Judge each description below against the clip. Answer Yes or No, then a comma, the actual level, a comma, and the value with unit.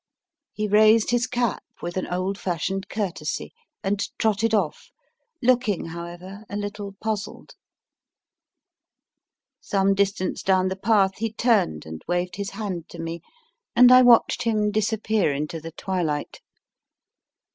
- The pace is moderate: No, slow, 130 wpm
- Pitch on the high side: Yes, high, 200 Hz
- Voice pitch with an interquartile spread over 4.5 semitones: No, average, 3.4 semitones